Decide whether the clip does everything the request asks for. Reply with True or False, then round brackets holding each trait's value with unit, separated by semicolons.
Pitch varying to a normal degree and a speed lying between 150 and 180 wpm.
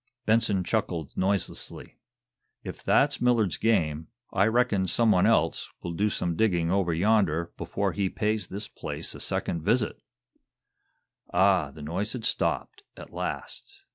False (4.4 semitones; 140 wpm)